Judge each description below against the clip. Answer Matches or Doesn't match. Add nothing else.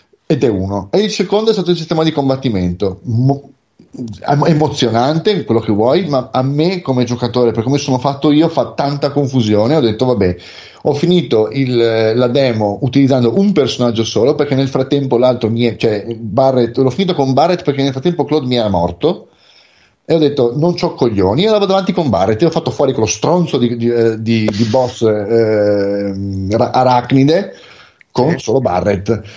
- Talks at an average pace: Doesn't match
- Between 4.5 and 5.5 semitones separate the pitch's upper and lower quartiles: Matches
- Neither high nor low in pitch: Doesn't match